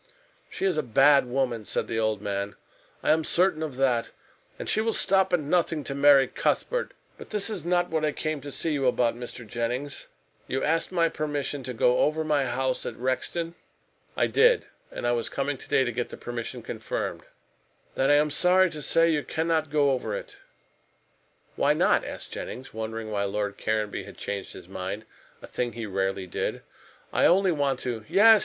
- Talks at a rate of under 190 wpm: No, average, 200 wpm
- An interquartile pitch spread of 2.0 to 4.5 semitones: No, wide, 5.4 semitones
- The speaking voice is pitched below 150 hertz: Yes, low, 135 Hz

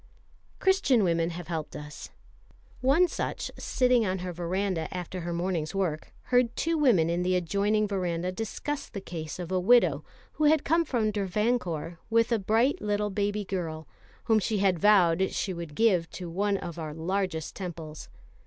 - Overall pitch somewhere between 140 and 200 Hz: Yes, high, 190 Hz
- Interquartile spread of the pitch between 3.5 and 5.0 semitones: Yes, average, 4.3 semitones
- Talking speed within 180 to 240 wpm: No, average, 170 wpm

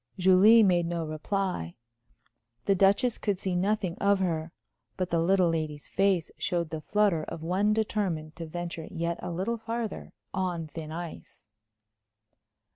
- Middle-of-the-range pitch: Yes, medium, 180 Hz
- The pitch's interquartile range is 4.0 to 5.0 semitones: No, average, 3.3 semitones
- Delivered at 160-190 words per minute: No, average, 145 wpm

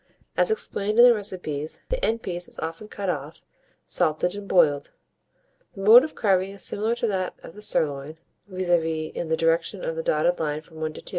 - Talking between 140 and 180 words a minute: No, fast, 205 wpm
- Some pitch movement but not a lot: Yes, average, 4.4 semitones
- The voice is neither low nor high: Yes, medium, 175 Hz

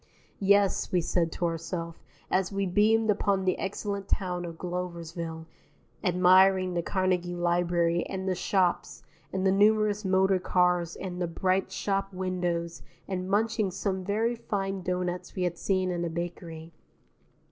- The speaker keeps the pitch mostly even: Yes, narrow, 1.9 semitones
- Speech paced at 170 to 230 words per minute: No, average, 145 wpm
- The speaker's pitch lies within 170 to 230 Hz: Yes, medium, 185 Hz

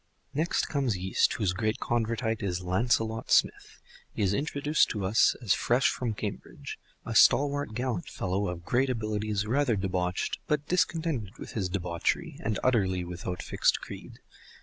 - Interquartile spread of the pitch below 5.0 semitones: No, average, 5.3 semitones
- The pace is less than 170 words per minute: Yes, average, 150 wpm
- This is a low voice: Yes, low, 110 Hz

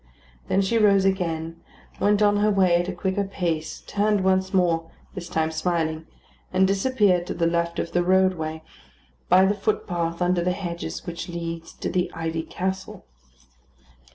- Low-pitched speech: No, medium, 180 Hz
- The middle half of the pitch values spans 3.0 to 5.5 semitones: No, narrow, 2.4 semitones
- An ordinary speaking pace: Yes, average, 160 wpm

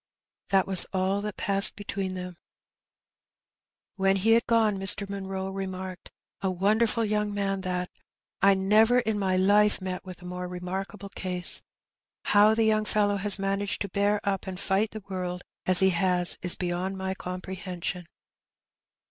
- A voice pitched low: No, high, 195 Hz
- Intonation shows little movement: Yes, narrow, 1.7 semitones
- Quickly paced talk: No, average, 165 wpm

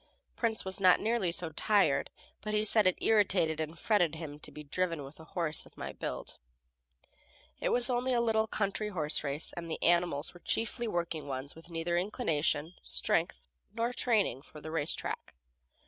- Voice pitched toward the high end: No, medium, 175 Hz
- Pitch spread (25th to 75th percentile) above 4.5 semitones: Yes, average, 5.2 semitones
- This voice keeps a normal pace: Yes, average, 180 wpm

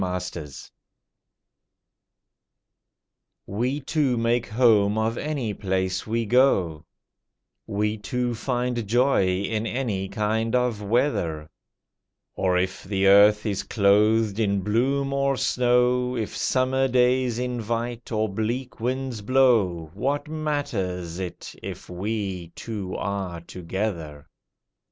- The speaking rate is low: Yes, slow, 110 wpm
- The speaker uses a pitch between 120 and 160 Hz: No, low, 110 Hz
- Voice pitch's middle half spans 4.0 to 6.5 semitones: Yes, average, 4.4 semitones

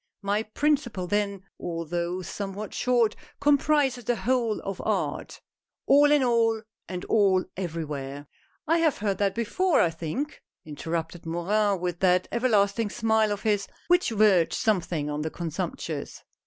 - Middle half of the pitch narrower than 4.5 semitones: No, average, 5.2 semitones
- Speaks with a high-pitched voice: Yes, high, 200 Hz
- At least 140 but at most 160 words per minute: Yes, average, 150 wpm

